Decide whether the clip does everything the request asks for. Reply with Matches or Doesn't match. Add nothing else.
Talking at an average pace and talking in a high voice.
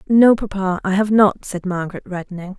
Matches